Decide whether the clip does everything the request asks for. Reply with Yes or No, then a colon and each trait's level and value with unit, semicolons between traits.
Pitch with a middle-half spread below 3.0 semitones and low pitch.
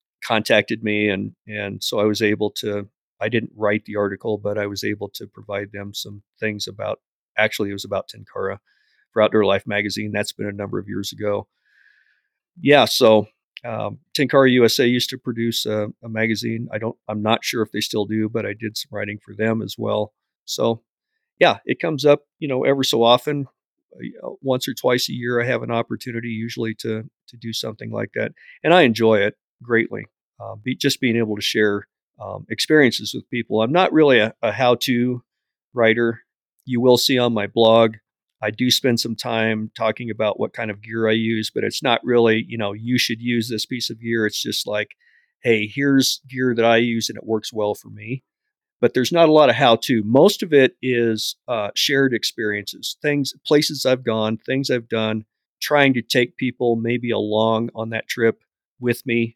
Yes: narrow, 2.6 semitones; low, 115 Hz